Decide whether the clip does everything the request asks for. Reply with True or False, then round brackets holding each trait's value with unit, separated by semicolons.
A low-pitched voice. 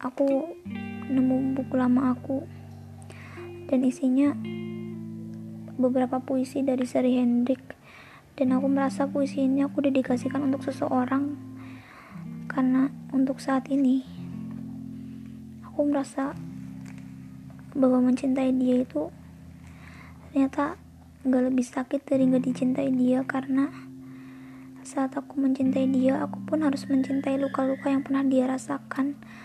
False (260 Hz)